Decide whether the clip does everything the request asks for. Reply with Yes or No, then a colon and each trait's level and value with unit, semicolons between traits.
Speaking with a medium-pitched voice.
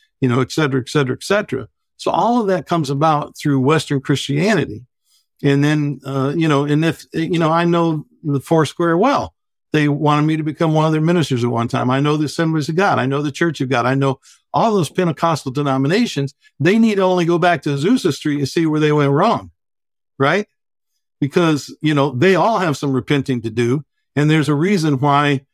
Yes: medium, 150 Hz